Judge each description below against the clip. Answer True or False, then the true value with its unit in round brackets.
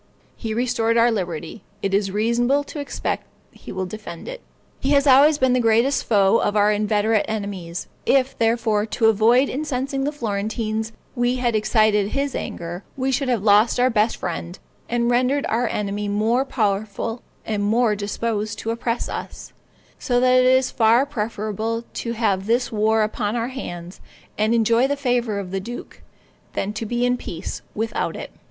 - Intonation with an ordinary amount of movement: True (3.0 semitones)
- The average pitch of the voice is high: True (225 Hz)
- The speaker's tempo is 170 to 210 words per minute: True (175 wpm)